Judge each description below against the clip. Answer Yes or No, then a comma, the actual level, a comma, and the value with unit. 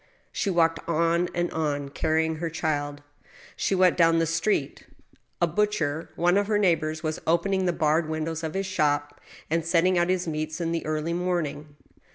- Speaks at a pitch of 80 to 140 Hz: No, medium, 165 Hz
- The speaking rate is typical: Yes, average, 180 wpm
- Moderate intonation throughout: No, narrow, 2.0 semitones